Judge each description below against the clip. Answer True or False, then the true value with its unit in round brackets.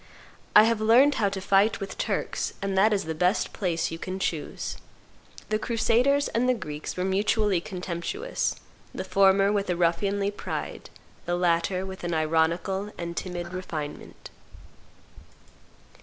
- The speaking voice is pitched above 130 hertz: True (190 Hz)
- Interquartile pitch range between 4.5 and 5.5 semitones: False (3.3 semitones)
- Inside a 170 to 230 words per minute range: False (145 wpm)